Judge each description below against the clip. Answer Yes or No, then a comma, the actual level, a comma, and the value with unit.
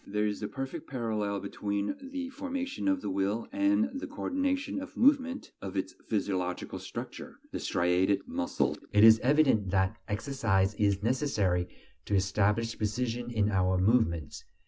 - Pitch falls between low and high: No, low, 110 Hz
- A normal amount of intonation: No, wide, 7.3 semitones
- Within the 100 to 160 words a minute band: Yes, average, 145 wpm